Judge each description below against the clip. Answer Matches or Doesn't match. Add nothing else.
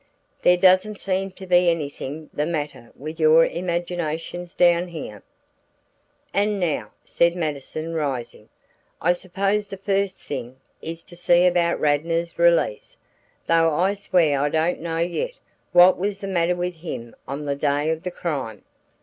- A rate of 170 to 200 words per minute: Doesn't match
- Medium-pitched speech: Matches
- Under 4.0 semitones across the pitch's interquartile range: Matches